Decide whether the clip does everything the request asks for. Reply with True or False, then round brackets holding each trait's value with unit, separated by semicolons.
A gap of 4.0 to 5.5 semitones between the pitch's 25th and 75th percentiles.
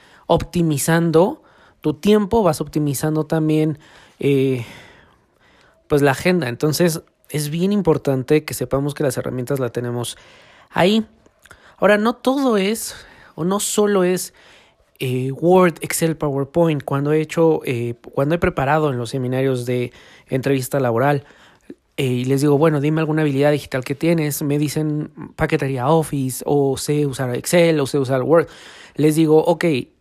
False (3.4 semitones)